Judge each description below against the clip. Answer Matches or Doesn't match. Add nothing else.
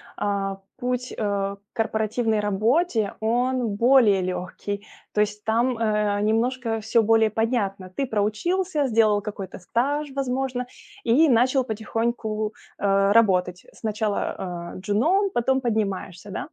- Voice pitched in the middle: Doesn't match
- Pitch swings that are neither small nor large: Matches